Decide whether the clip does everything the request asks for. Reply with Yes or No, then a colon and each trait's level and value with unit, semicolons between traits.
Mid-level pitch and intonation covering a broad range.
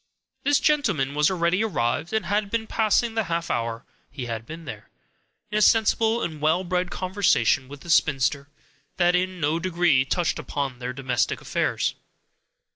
Yes: medium, 170 Hz; wide, 6.8 semitones